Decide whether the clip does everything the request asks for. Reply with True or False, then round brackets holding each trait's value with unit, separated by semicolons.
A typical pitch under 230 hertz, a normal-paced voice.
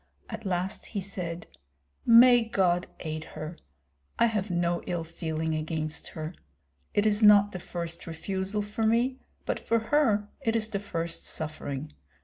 True (185 Hz; 150 wpm)